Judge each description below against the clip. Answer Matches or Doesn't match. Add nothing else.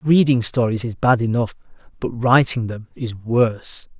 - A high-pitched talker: Doesn't match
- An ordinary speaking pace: Matches